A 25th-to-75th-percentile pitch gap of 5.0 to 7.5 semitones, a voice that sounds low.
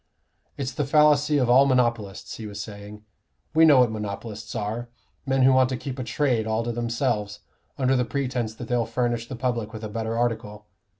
No: average, 2.9 semitones; low, 120 Hz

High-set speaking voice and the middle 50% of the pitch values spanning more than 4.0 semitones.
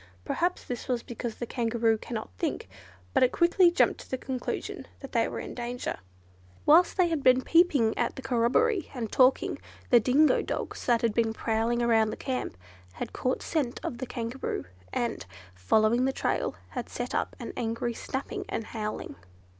No: high, 240 Hz; average, 2.8 semitones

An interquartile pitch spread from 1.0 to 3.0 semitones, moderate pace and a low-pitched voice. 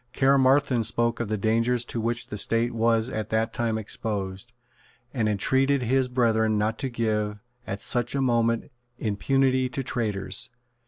Yes: narrow, 2.5 semitones; average, 155 wpm; low, 115 Hz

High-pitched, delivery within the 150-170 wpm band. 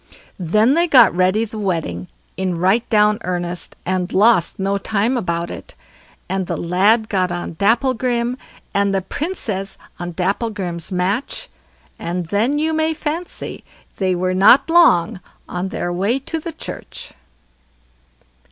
No: high, 200 Hz; average, 140 wpm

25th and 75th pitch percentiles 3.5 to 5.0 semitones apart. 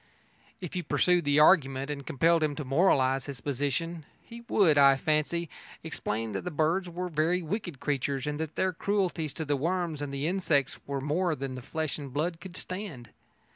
Yes: average, 3.9 semitones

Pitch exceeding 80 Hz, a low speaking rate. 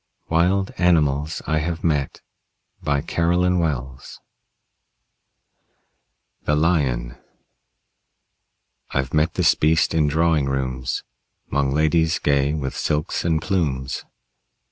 No: very low, 75 Hz; slow, 100 wpm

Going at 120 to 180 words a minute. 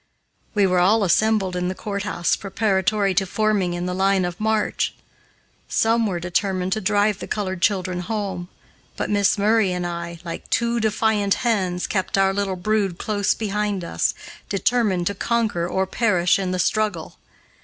Yes: average, 165 wpm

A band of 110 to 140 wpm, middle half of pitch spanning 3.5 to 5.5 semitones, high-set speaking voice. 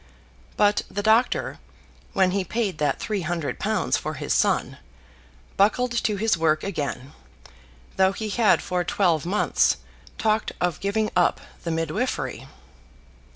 Yes: slow, 135 wpm; average, 4.2 semitones; high, 195 Hz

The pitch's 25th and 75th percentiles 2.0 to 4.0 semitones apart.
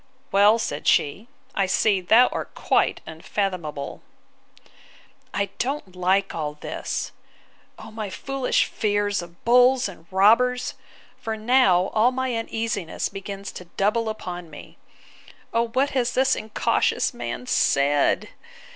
No: average, 4.5 semitones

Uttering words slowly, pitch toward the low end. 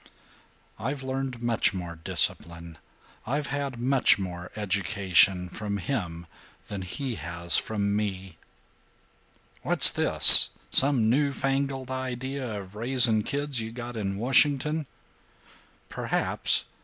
Yes: slow, 110 wpm; low, 115 Hz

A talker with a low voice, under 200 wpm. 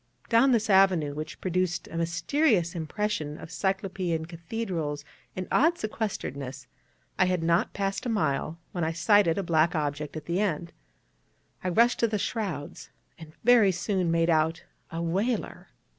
No: medium, 175 Hz; average, 155 wpm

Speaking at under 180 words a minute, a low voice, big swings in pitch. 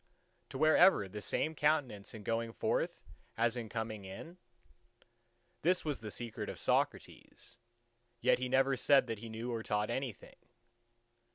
No: average, 155 wpm; low, 115 Hz; average, 3.9 semitones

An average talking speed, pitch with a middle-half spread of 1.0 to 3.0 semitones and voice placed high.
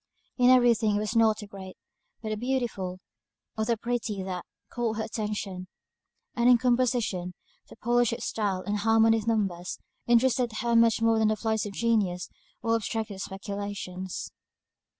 Yes: average, 165 wpm; average, 2.7 semitones; high, 220 Hz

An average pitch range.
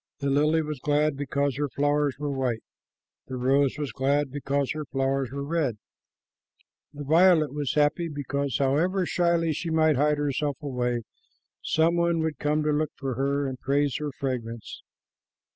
No: narrow, 2.1 semitones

